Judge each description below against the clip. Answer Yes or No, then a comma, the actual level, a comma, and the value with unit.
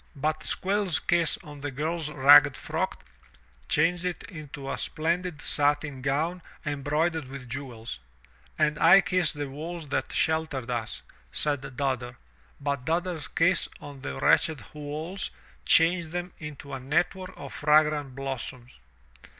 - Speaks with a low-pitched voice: No, medium, 150 Hz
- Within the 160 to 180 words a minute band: No, slow, 135 wpm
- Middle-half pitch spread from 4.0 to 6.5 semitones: No, average, 3.3 semitones